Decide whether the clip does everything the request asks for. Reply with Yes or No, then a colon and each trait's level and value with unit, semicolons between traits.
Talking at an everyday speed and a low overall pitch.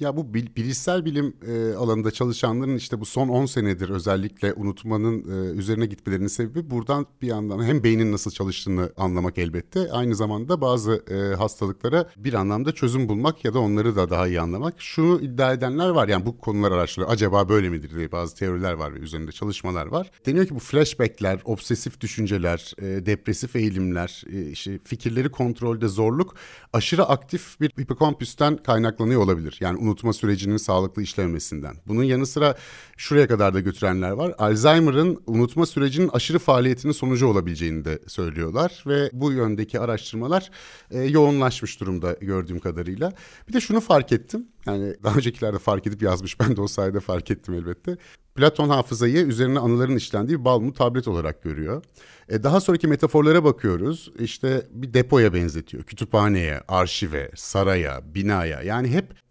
No: fast, 150 wpm; low, 115 Hz